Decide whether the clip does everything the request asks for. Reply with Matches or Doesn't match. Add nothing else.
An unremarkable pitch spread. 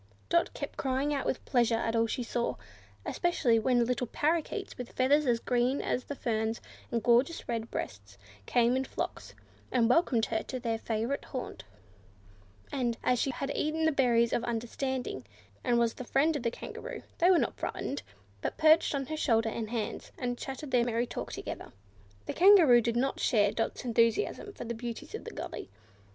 Matches